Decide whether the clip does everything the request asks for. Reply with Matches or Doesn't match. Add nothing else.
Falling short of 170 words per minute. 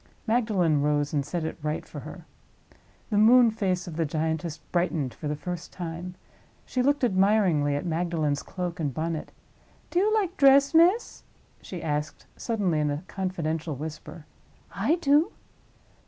Matches